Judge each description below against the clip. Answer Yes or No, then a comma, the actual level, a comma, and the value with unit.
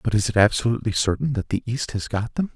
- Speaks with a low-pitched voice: Yes, low, 110 Hz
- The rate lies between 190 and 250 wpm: No, fast, 260 wpm